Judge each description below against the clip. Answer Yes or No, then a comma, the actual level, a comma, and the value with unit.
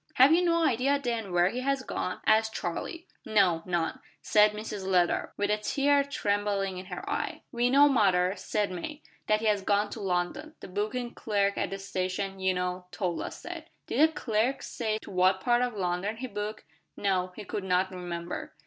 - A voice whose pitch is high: Yes, high, 210 Hz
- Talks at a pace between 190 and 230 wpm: Yes, average, 195 wpm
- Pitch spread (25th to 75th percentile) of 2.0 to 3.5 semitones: No, average, 5.0 semitones